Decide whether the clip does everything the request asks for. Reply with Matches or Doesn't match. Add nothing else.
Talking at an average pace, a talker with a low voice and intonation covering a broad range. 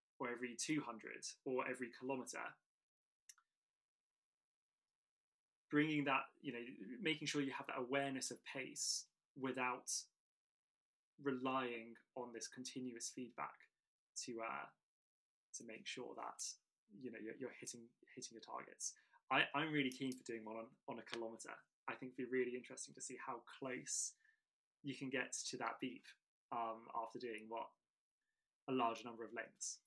Doesn't match